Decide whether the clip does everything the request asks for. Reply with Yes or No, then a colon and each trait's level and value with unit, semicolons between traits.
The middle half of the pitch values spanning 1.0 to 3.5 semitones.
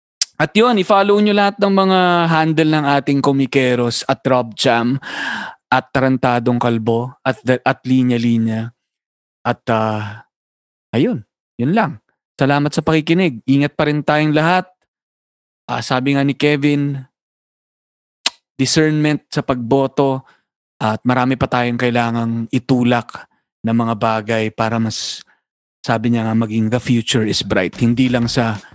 No: average, 4.1 semitones